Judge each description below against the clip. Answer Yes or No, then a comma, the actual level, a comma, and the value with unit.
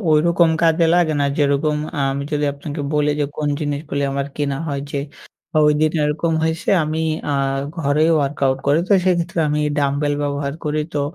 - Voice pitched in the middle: Yes, medium, 150 Hz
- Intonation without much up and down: Yes, narrow, 1.9 semitones